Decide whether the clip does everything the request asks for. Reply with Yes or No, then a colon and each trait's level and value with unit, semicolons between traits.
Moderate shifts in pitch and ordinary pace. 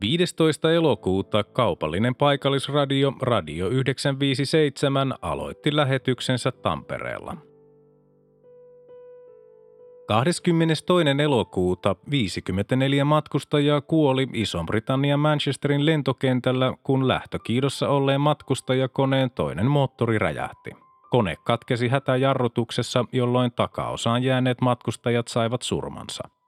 No: average, 3.2 semitones; slow, 75 wpm